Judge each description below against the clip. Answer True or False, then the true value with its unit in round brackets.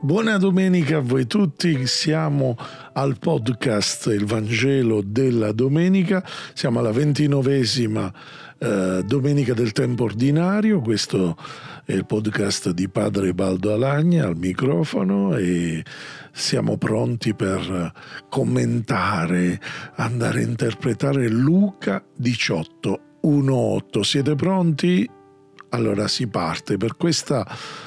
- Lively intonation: True (6.6 semitones)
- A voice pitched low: True (125 Hz)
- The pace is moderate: False (100 wpm)